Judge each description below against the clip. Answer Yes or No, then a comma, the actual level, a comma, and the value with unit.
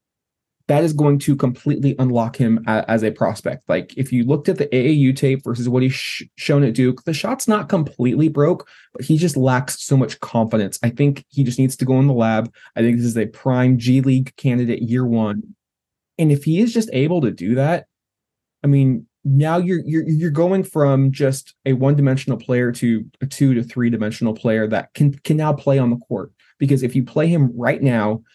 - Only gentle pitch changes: No, average, 3.3 semitones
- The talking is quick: Yes, fast, 215 wpm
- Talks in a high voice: No, low, 130 Hz